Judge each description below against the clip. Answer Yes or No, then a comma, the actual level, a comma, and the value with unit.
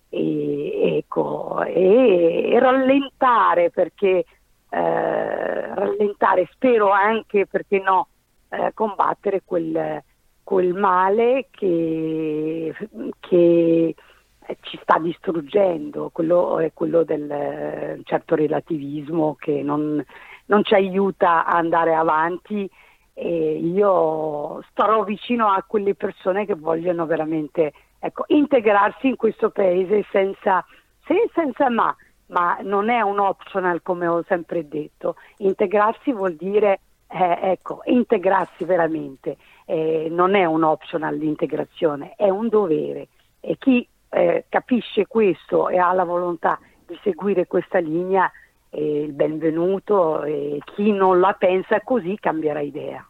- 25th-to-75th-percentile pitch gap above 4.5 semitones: No, average, 4.2 semitones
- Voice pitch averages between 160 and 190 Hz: Yes, medium, 185 Hz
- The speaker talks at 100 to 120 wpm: Yes, slow, 115 wpm